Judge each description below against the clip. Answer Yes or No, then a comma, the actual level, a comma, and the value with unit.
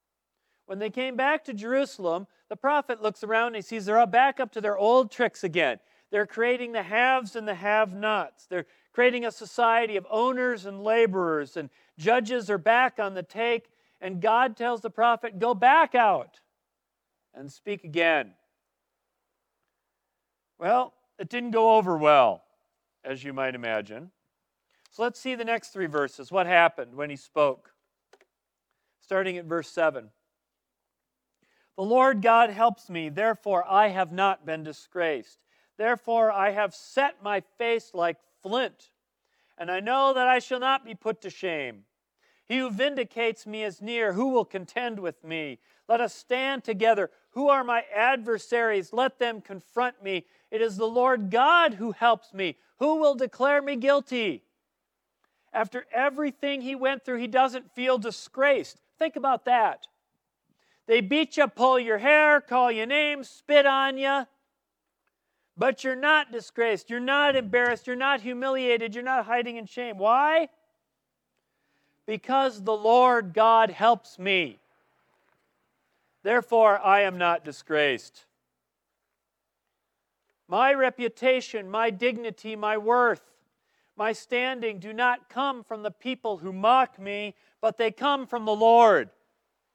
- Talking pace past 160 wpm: No, average, 150 wpm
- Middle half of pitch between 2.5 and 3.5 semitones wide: No, average, 4.3 semitones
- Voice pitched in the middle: No, high, 230 Hz